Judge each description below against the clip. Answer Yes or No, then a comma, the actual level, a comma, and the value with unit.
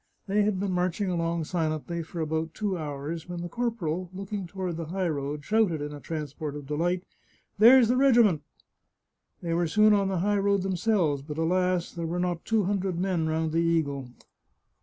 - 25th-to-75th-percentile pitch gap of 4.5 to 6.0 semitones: No, average, 3.5 semitones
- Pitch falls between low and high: Yes, medium, 175 Hz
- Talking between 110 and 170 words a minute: No, average, 195 wpm